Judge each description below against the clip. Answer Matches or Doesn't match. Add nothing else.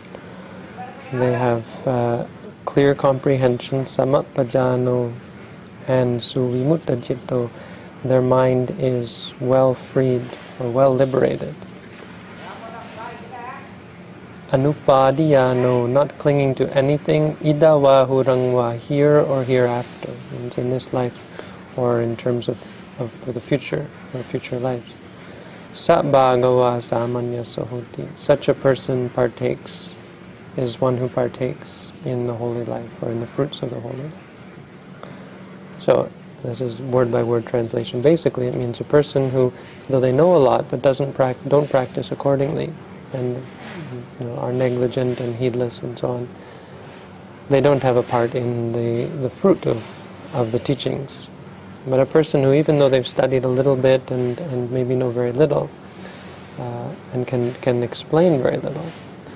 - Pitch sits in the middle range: Doesn't match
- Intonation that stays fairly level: Matches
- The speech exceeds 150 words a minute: Doesn't match